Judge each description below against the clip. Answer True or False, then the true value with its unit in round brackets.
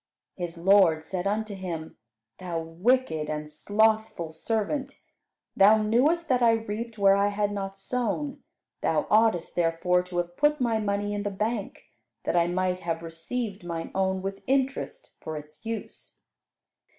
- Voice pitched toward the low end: False (200 Hz)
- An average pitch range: True (4.3 semitones)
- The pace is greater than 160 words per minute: False (150 wpm)